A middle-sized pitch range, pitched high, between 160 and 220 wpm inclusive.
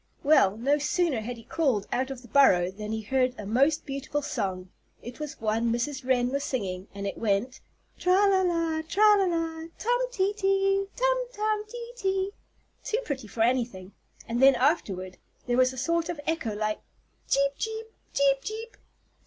No: wide, 8.5 semitones; very high, 275 Hz; average, 185 wpm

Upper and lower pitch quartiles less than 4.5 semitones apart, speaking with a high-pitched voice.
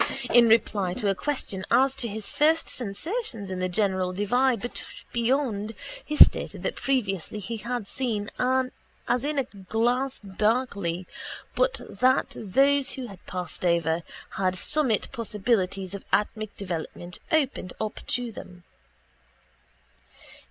No: average, 5.1 semitones; high, 220 Hz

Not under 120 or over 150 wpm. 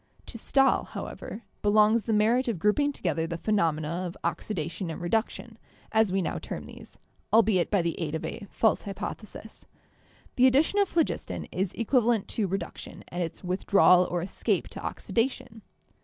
No: average, 165 wpm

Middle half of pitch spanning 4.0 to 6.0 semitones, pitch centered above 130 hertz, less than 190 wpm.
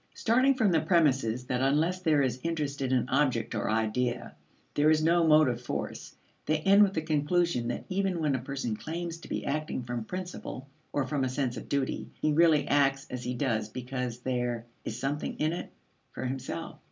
No: average, 4.4 semitones; medium, 140 Hz; average, 195 wpm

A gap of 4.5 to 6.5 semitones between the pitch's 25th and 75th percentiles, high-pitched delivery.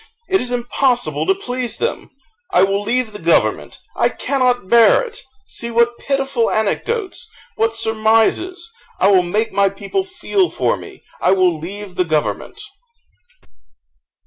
Yes: wide, 5.4 semitones; high, 230 Hz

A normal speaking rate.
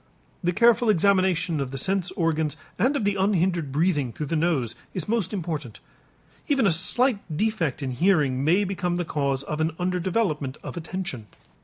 Yes: average, 175 wpm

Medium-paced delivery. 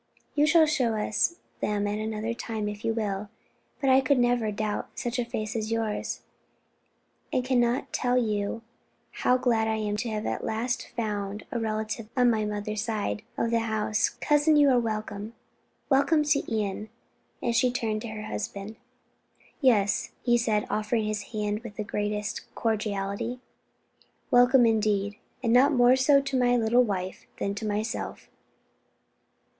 Yes: average, 160 wpm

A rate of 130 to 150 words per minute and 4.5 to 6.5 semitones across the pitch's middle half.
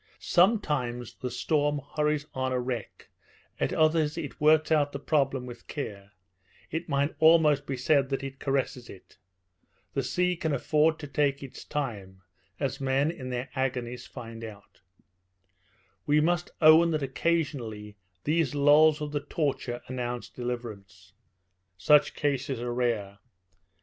No: average, 140 wpm; average, 3.7 semitones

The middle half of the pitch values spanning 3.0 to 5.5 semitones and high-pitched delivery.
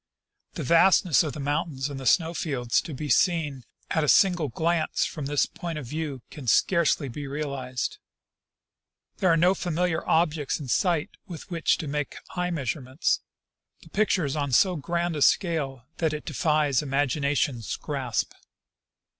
No: average, 3.5 semitones; medium, 150 Hz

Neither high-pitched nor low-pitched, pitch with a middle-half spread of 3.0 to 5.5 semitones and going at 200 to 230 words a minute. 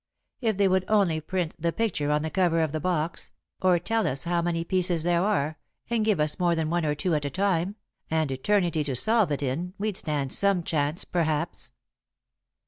Yes: medium, 170 Hz; average, 3.6 semitones; fast, 205 wpm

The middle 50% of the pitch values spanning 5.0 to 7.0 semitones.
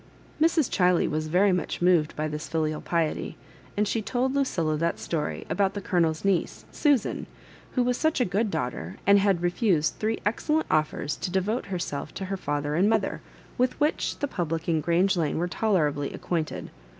Yes: wide, 5.4 semitones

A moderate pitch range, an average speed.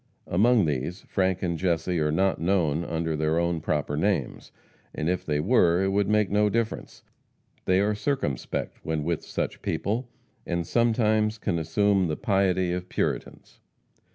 Yes: average, 4.2 semitones; average, 155 wpm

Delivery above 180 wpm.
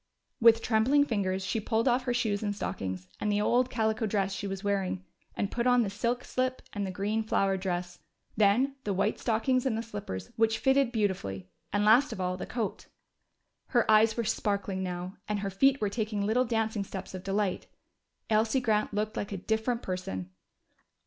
Yes: average, 190 wpm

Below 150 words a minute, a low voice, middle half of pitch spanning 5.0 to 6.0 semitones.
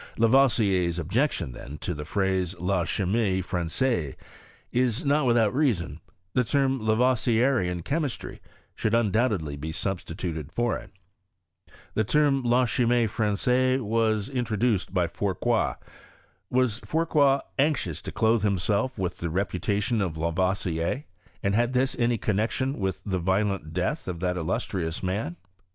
Yes: slow, 135 wpm; low, 105 Hz; wide, 5.5 semitones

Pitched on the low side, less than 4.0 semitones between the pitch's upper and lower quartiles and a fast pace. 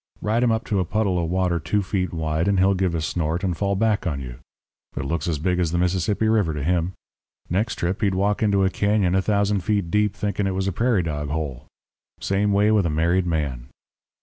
Yes: very low, 95 Hz; average, 3.6 semitones; fast, 230 wpm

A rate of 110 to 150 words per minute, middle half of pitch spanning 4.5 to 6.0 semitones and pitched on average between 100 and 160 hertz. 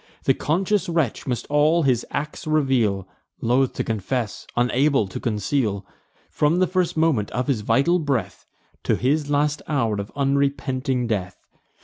Yes: average, 145 wpm; average, 4.8 semitones; low, 135 Hz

